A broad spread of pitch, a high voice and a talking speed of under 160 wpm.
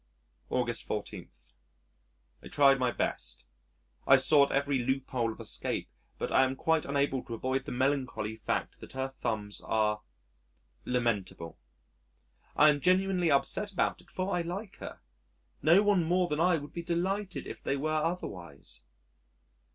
No: wide, 5.8 semitones; medium, 140 Hz; average, 150 wpm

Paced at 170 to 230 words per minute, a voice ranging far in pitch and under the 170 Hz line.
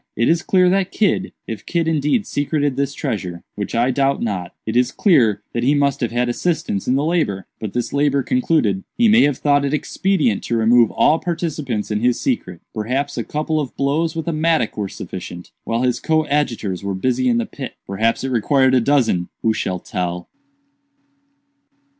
Yes: average, 185 wpm; wide, 5.9 semitones; low, 135 Hz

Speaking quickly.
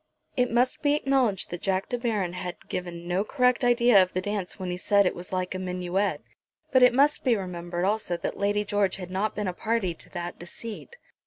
Yes: fast, 225 wpm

